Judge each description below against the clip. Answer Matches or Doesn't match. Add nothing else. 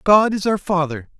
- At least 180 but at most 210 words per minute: Matches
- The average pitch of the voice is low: Doesn't match